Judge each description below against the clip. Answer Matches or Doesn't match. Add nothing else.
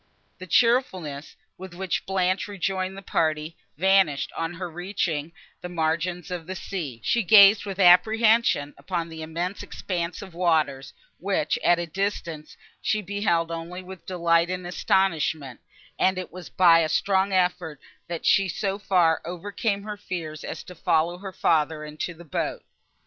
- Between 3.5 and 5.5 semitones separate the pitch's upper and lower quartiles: Doesn't match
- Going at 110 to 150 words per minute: Doesn't match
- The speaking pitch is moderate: Matches